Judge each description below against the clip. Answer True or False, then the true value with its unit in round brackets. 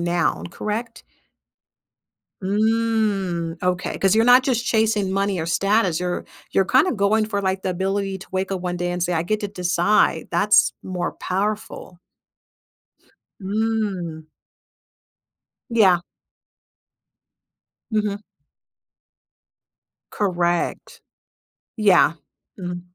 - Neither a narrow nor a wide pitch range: True (3.2 semitones)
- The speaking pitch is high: True (195 Hz)